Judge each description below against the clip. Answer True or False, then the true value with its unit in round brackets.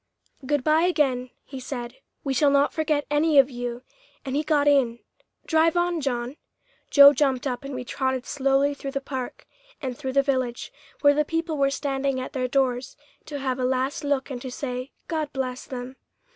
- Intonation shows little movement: True (2.2 semitones)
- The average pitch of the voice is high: True (275 Hz)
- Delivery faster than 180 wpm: True (190 wpm)